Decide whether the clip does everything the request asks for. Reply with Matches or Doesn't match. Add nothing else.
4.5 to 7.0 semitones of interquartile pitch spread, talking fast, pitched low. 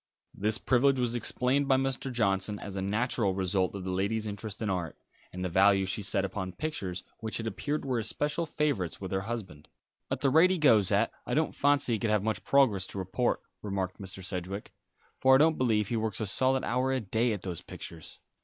Matches